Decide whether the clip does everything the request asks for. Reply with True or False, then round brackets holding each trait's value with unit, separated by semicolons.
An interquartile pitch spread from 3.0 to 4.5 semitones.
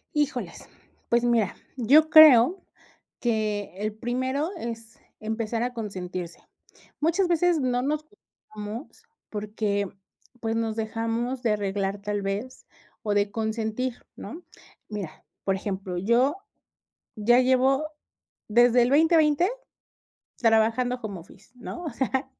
True (3.8 semitones)